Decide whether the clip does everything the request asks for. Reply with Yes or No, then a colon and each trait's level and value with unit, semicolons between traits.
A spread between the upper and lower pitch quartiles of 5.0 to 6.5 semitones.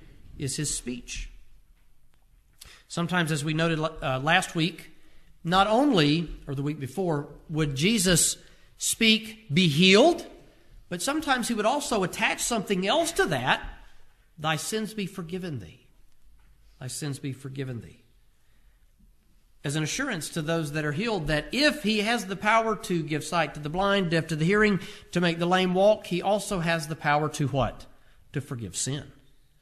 Yes: wide, 5.5 semitones